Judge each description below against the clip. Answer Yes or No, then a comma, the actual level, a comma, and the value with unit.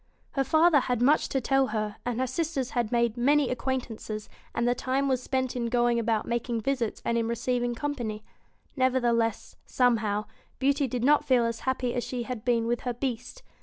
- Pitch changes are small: Yes, narrow, 2.1 semitones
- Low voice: No, high, 245 Hz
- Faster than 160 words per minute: Yes, average, 195 wpm